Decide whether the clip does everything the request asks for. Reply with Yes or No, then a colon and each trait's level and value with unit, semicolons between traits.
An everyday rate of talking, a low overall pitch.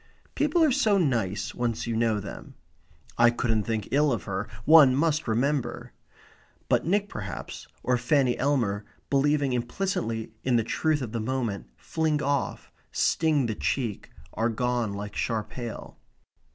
Yes: average, 150 wpm; low, 125 Hz